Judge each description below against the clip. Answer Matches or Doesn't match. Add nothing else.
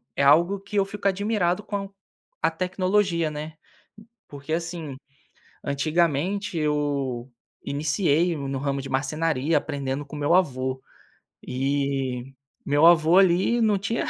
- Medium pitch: Matches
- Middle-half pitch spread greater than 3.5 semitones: Matches